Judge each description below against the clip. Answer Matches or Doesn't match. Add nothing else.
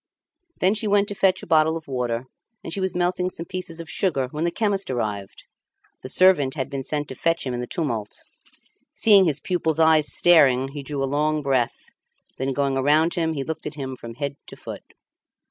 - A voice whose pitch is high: Doesn't match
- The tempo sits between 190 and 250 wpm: Matches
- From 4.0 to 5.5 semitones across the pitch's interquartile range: Matches